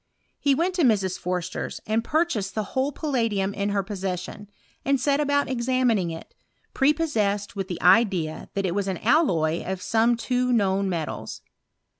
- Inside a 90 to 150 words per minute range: No, average, 160 wpm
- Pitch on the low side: No, high, 210 Hz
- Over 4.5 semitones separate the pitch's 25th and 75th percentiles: Yes, wide, 5.5 semitones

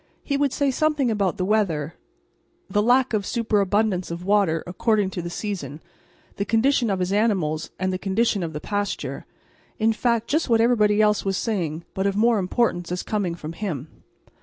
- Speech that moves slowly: No, average, 185 wpm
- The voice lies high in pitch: Yes, high, 205 Hz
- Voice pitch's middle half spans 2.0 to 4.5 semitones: Yes, average, 3.9 semitones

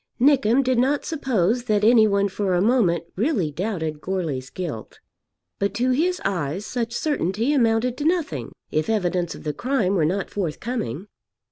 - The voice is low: No, high, 210 Hz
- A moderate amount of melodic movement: No, wide, 6.2 semitones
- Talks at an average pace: Yes, average, 160 wpm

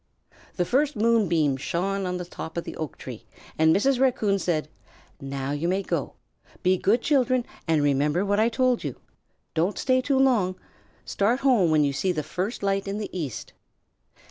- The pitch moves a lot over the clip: Yes, wide, 6.6 semitones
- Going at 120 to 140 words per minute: No, average, 180 wpm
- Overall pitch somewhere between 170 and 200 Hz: Yes, high, 190 Hz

